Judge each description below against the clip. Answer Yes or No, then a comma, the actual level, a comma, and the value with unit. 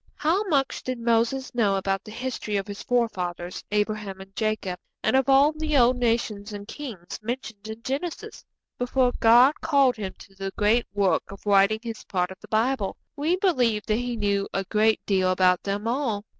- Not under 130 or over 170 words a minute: No, average, 185 wpm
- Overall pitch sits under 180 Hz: No, high, 220 Hz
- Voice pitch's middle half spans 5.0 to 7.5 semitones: No, average, 4.3 semitones